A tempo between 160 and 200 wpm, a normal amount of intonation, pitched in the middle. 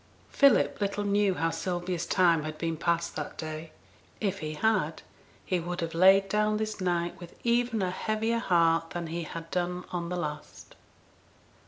Yes: average, 170 wpm; average, 3.4 semitones; medium, 180 Hz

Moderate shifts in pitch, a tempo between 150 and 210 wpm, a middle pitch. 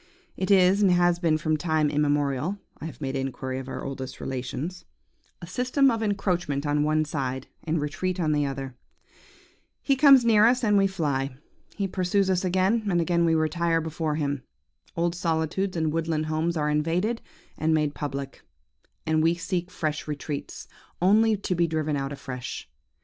Yes: average, 3.9 semitones; average, 170 wpm; medium, 160 Hz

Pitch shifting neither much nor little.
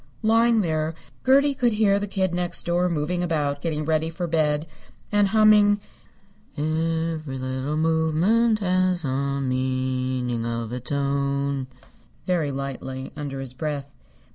Yes: average, 4.8 semitones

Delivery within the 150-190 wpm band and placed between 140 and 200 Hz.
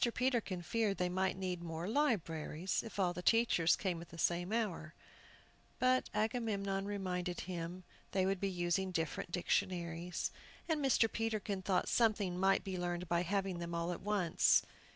Yes: average, 165 wpm; medium, 185 Hz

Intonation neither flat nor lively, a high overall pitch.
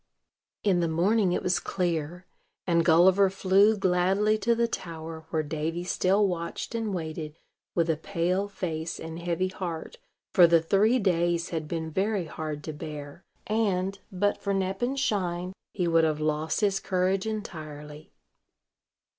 No: average, 3.3 semitones; medium, 175 Hz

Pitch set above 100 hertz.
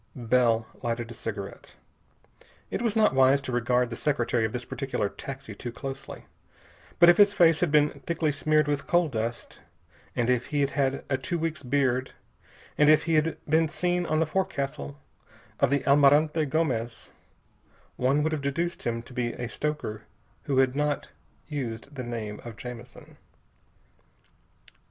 Yes: medium, 140 Hz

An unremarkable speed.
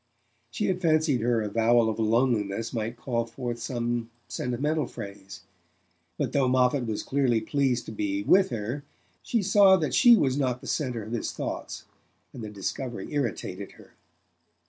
Yes: average, 160 wpm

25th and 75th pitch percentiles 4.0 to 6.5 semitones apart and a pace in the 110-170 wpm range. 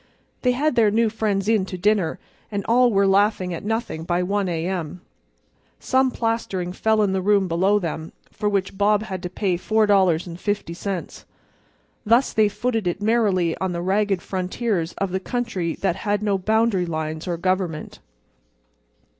No: average, 3.3 semitones; average, 165 wpm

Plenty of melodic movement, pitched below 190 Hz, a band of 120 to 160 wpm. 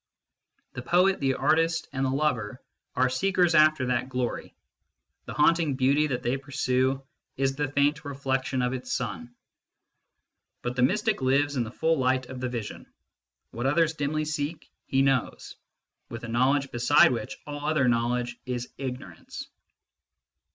No: average, 2.9 semitones; low, 135 Hz; average, 150 wpm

